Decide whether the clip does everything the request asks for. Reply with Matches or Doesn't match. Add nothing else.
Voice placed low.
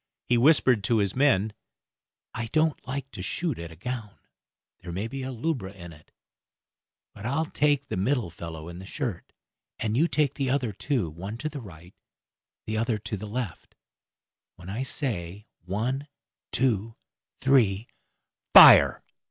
Matches